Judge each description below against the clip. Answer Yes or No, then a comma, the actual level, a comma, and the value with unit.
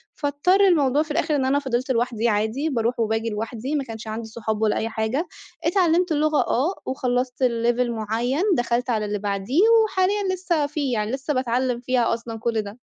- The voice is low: No, very high, 250 Hz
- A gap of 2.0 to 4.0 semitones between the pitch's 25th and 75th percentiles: No, average, 4.6 semitones